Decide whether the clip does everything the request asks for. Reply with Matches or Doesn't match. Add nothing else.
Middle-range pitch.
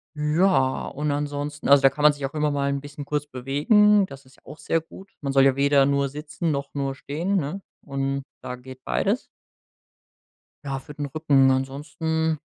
Matches